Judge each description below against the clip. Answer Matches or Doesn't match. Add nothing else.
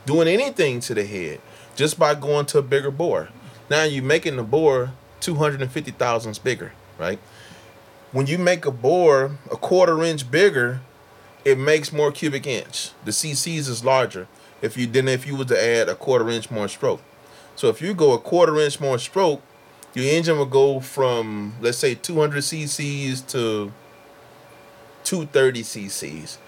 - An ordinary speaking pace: Matches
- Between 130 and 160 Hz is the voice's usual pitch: Matches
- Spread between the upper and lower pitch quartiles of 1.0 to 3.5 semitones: Doesn't match